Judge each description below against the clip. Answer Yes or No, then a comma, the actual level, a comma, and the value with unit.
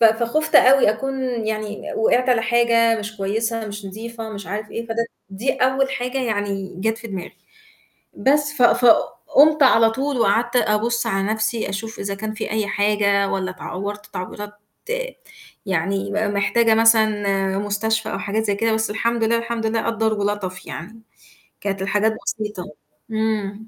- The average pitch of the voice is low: No, high, 220 Hz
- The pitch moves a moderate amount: No, narrow, 2.3 semitones